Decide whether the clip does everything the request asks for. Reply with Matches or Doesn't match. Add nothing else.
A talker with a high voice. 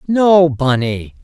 Doesn't match